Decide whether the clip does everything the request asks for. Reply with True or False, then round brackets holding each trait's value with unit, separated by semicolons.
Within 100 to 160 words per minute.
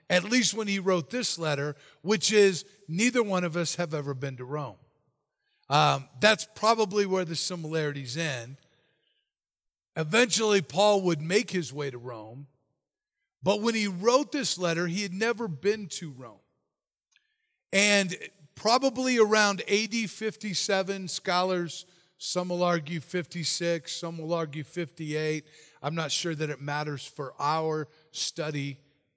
True (140 wpm)